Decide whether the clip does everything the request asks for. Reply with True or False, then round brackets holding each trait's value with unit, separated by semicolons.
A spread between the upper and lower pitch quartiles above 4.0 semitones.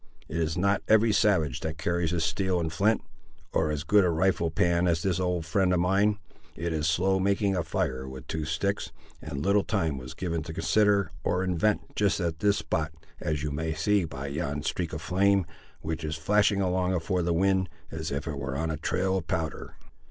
False (3.3 semitones)